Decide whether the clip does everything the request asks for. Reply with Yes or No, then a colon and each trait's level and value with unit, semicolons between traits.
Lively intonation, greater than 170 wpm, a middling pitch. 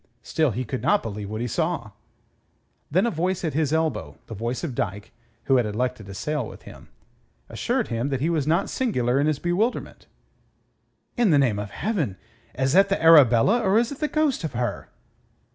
Yes: wide, 7.1 semitones; average, 200 wpm; medium, 145 Hz